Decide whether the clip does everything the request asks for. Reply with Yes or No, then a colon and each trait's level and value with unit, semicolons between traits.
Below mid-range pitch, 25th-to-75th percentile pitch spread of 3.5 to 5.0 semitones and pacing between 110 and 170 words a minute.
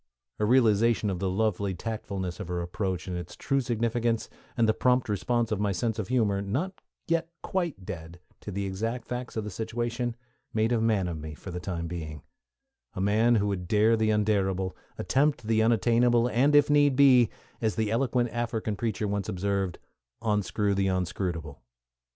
No: low, 110 Hz; average, 3.9 semitones; average, 180 wpm